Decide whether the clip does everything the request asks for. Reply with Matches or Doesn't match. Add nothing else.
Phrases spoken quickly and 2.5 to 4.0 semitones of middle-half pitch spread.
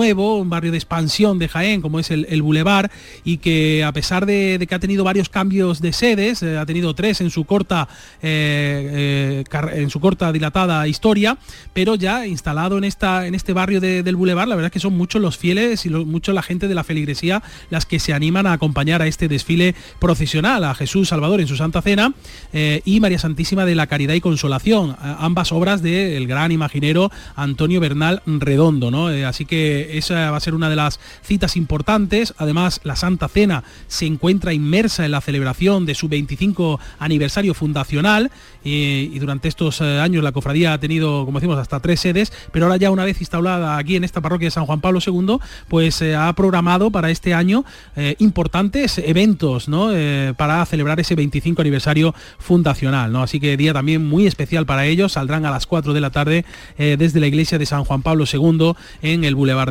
Matches